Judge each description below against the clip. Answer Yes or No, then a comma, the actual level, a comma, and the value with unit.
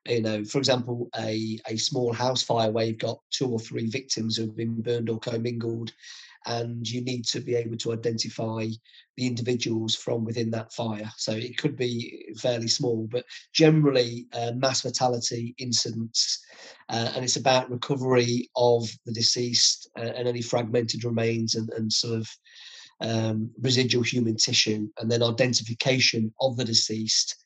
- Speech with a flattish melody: Yes, narrow, 1.6 semitones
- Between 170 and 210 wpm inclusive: No, average, 160 wpm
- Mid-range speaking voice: No, low, 120 Hz